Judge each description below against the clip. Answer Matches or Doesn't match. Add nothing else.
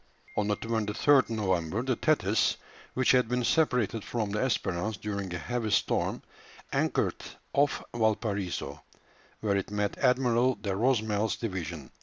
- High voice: Doesn't match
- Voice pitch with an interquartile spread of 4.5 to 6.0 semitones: Doesn't match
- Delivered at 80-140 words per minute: Matches